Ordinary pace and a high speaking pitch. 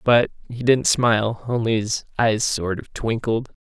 No: average, 165 wpm; low, 115 Hz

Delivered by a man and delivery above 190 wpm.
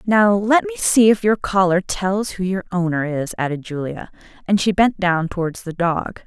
No: female; average, 200 wpm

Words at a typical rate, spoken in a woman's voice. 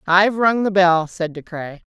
No: fast, 220 wpm; female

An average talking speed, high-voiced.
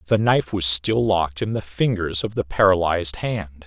No: average, 195 wpm; very low, 95 Hz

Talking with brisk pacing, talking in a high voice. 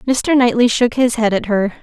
Yes: fast, 230 wpm; high, 235 Hz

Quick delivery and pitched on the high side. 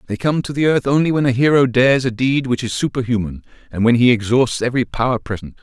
No: fast, 235 wpm; low, 125 Hz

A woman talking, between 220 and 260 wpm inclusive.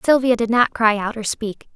Yes: female; fast, 240 wpm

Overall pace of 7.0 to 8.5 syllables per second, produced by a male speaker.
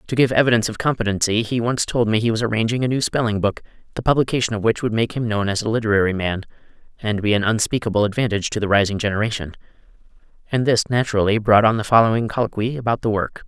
Yes: 7.1 syllables/s; male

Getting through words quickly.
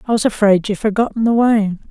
Yes: fast, 220 wpm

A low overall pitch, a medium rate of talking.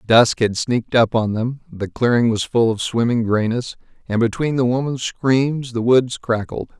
Yes: low, 120 Hz; average, 185 wpm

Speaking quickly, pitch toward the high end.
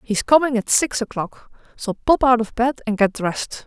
Yes: fast, 230 wpm; high, 235 Hz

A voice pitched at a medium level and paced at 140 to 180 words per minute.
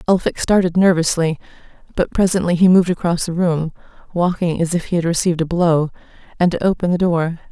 Yes: medium, 170 Hz; average, 175 wpm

